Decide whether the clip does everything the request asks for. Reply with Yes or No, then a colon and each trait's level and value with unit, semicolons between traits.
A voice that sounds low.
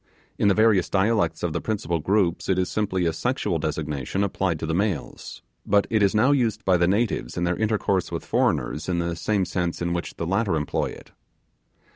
Yes: very low, 95 Hz